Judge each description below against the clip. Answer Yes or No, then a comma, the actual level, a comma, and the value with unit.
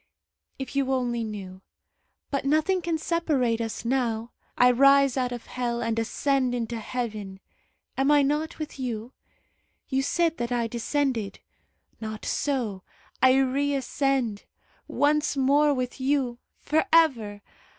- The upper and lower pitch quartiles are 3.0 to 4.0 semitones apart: Yes, average, 3.5 semitones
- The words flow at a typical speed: No, slow, 130 wpm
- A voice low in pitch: No, very high, 255 Hz